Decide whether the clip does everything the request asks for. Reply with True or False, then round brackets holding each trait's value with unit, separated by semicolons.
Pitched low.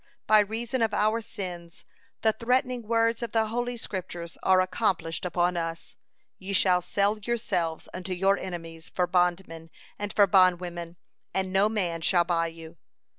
False (185 Hz)